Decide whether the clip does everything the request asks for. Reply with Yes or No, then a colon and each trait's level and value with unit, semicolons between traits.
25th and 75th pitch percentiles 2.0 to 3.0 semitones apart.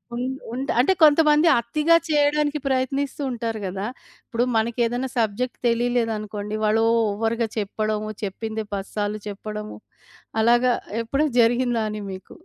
No: average, 3.4 semitones